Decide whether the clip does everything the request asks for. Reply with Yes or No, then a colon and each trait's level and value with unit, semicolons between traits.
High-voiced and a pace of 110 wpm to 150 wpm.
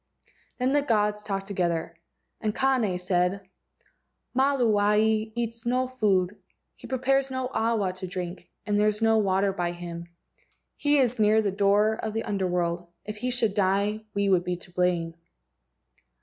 No: high, 210 Hz; average, 160 wpm